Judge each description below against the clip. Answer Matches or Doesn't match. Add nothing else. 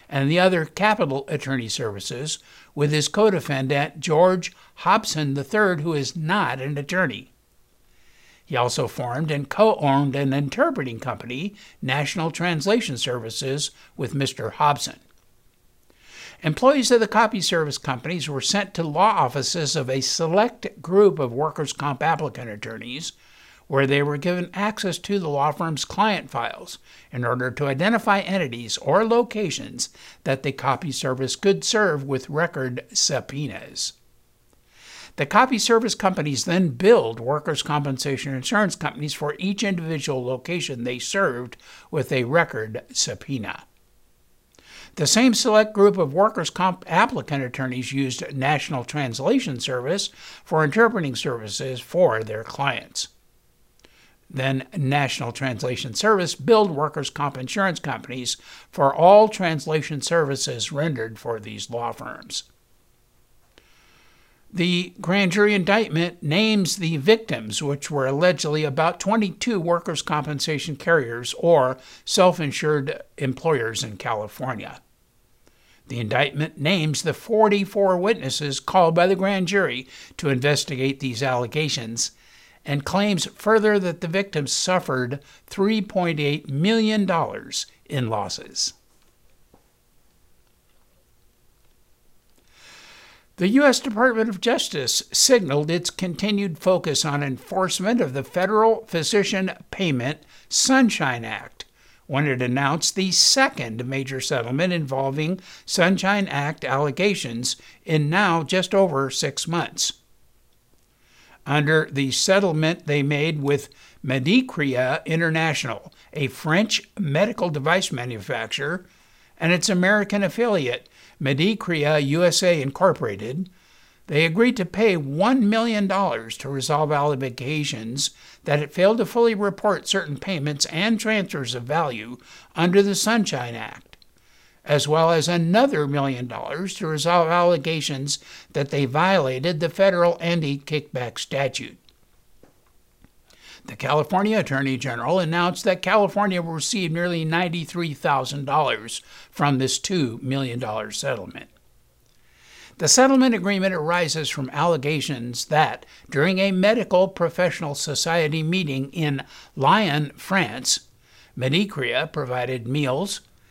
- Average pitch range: Doesn't match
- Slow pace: Matches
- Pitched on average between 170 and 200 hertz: Doesn't match